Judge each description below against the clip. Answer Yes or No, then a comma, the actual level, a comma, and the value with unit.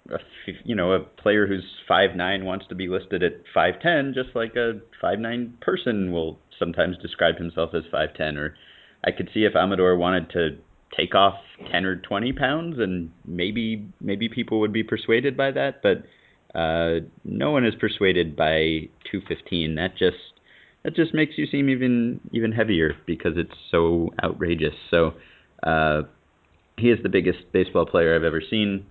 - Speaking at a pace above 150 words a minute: Yes, average, 165 wpm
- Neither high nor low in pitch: No, very low, 95 Hz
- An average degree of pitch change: No, wide, 5.7 semitones